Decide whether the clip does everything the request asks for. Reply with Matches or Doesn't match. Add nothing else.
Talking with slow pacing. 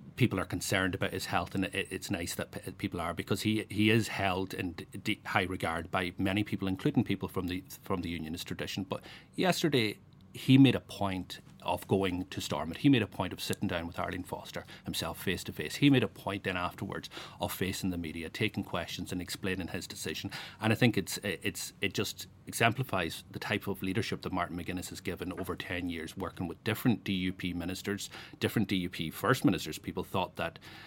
Doesn't match